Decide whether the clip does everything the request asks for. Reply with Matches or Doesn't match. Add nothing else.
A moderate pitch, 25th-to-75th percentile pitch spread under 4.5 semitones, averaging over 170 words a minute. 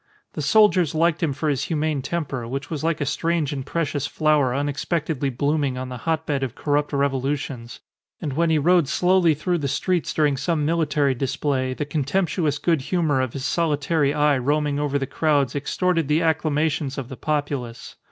Matches